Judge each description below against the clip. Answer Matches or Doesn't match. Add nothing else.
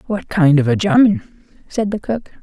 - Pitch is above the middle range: Matches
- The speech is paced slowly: Doesn't match